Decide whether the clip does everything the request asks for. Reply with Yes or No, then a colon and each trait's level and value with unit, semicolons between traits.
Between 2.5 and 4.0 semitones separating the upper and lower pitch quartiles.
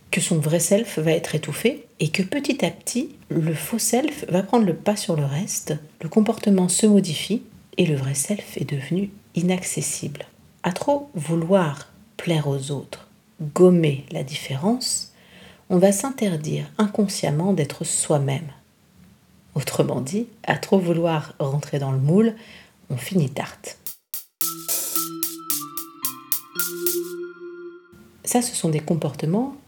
No: wide, 5.6 semitones